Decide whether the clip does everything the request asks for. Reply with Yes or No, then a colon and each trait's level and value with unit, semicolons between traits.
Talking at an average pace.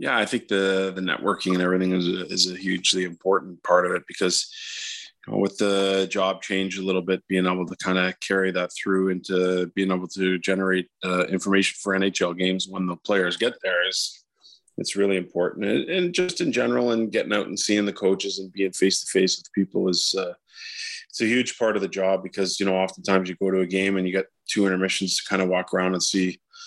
No: fast, 230 wpm